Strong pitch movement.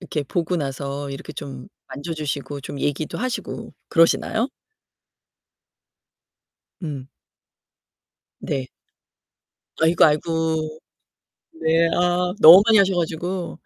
No: average, 3.5 semitones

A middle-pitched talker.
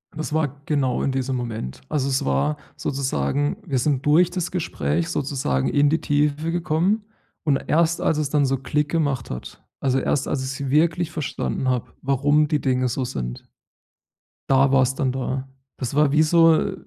Yes: medium, 145 Hz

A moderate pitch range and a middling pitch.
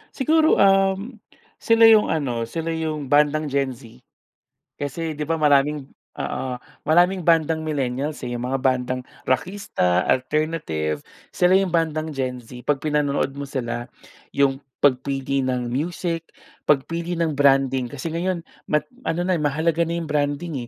Yes: average, 4.0 semitones; medium, 150 Hz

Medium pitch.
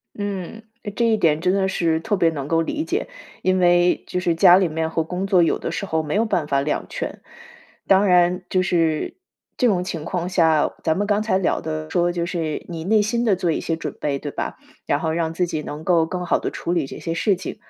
Yes: medium, 175 Hz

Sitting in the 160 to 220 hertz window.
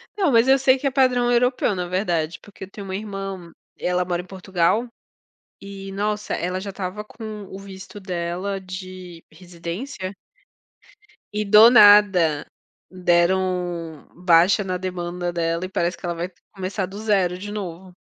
Yes: high, 190 Hz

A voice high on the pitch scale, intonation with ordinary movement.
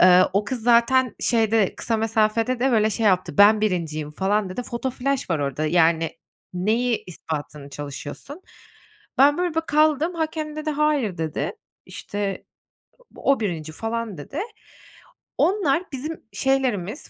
No: high, 225 Hz; wide, 7.0 semitones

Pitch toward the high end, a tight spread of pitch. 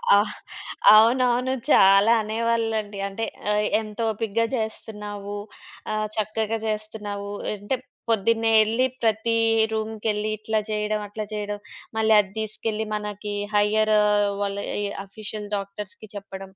Yes: high, 215 Hz; narrow, 1.2 semitones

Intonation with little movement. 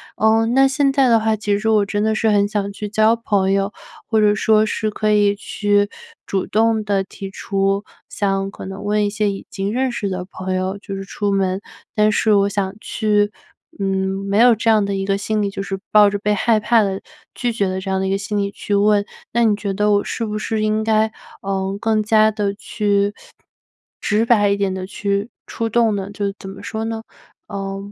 Yes: narrow, 1.7 semitones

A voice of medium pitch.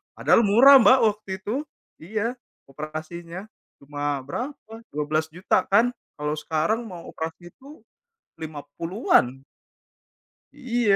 Yes: medium, 175 Hz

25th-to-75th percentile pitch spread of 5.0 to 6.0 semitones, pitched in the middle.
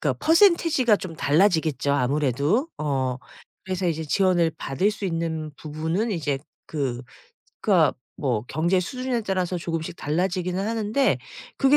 Yes: wide, 5.4 semitones; medium, 170 Hz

